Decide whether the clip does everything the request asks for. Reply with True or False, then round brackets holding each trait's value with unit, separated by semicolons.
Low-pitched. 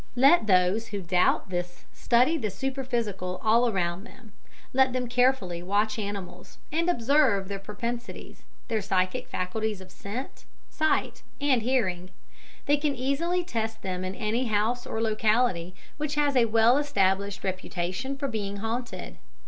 False (220 Hz)